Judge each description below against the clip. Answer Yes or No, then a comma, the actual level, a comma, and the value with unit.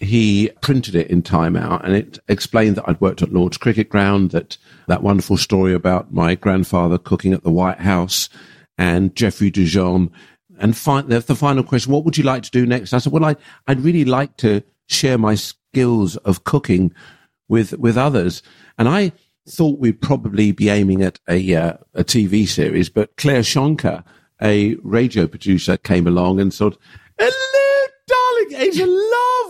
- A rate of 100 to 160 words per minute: No, average, 180 wpm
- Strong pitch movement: Yes, wide, 6.9 semitones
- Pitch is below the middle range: Yes, low, 105 Hz